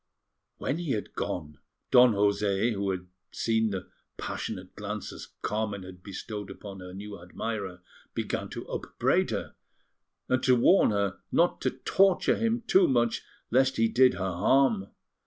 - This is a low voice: Yes, low, 105 Hz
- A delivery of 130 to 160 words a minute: Yes, average, 150 wpm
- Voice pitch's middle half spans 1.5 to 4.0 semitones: No, average, 4.4 semitones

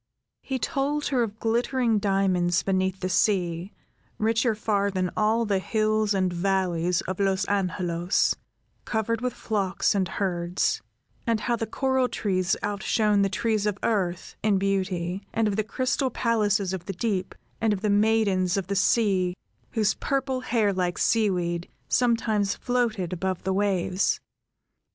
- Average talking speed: Yes, average, 150 wpm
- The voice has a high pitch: Yes, high, 200 Hz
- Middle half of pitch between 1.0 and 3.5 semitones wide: Yes, average, 3.1 semitones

